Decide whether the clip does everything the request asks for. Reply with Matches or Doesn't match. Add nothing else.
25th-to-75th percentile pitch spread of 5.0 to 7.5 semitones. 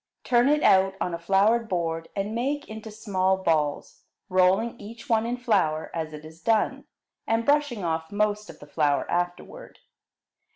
Matches